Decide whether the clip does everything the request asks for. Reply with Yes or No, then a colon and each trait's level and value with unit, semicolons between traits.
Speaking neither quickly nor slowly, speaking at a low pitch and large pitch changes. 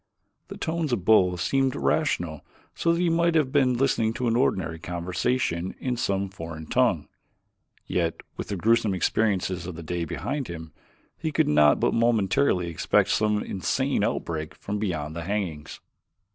Yes: average, 160 wpm; very low, 95 Hz; wide, 6.6 semitones